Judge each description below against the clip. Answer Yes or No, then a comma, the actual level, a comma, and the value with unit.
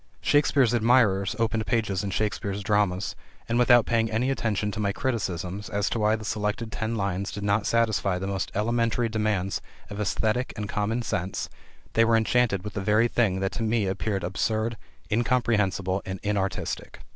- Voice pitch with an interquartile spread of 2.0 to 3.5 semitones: Yes, average, 2.7 semitones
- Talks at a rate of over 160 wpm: Yes, average, 170 wpm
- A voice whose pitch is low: Yes, low, 105 Hz